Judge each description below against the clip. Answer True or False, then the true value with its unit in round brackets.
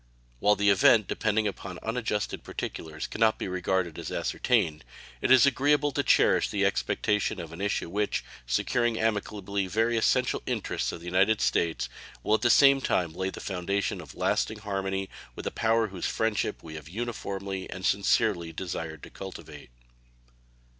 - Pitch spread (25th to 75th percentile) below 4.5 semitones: True (3.4 semitones)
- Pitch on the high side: False (100 Hz)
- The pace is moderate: True (165 wpm)